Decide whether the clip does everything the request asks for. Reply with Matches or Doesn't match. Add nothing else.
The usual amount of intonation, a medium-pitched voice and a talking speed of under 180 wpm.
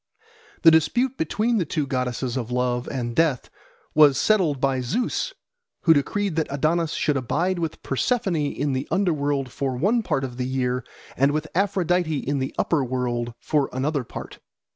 Matches